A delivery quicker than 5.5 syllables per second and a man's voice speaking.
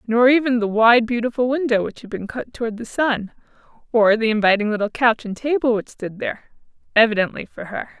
No: 5.7 syllables/s; female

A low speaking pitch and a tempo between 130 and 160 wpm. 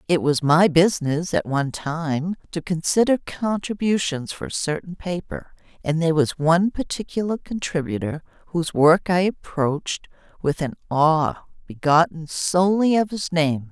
No: medium, 165 Hz; average, 140 wpm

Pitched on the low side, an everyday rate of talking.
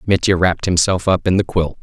No: very low, 90 Hz; fast, 230 wpm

